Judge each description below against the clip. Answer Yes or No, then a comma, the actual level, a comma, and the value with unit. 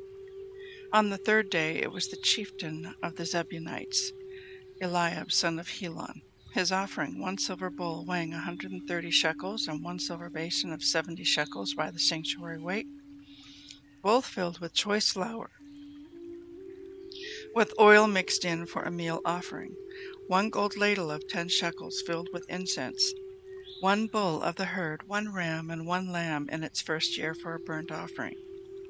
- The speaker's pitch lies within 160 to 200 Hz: Yes, medium, 185 Hz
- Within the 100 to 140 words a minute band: No, average, 155 wpm